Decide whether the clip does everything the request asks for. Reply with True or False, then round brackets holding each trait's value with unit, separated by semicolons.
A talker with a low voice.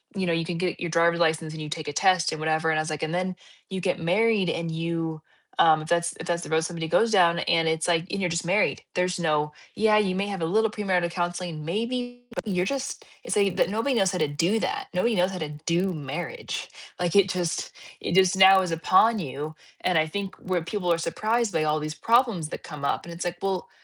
False (175 Hz)